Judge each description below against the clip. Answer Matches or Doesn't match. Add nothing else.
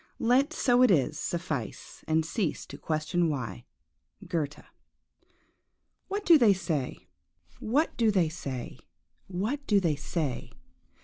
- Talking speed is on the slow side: Matches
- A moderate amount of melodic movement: Doesn't match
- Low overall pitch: Doesn't match